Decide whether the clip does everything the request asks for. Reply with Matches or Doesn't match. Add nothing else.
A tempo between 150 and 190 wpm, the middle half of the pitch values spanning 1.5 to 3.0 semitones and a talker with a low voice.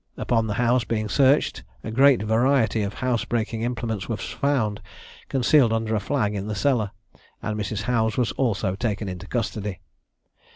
Matches